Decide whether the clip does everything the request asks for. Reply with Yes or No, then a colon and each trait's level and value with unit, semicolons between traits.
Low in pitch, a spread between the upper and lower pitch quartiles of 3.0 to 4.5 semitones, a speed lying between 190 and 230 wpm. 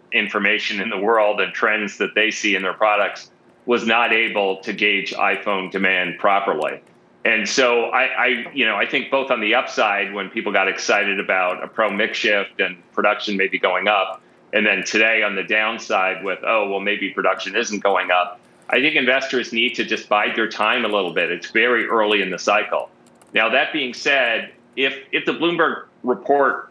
Yes: low, 105 Hz; average, 3.8 semitones; average, 195 wpm